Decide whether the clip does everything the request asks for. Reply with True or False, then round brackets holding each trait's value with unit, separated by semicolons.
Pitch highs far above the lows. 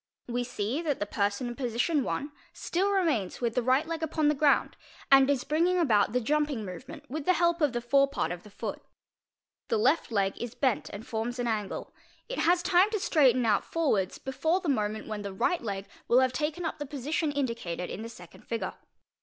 True (5.9 semitones)